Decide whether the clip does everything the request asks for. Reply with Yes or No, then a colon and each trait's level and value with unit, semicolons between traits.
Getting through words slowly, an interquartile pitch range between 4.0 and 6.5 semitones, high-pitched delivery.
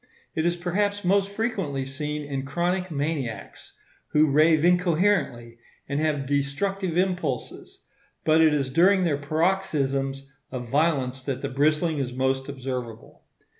No: slow, 130 wpm; average, 4.5 semitones; medium, 150 Hz